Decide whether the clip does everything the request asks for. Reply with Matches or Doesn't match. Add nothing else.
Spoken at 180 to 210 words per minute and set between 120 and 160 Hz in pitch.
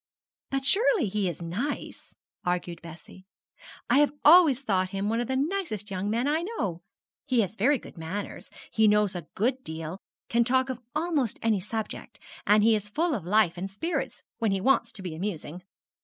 Doesn't match